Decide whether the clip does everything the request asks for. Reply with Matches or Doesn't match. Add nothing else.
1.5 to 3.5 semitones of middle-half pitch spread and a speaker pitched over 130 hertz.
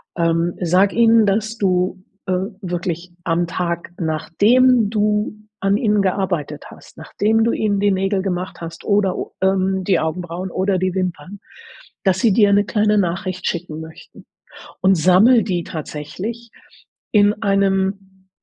Matches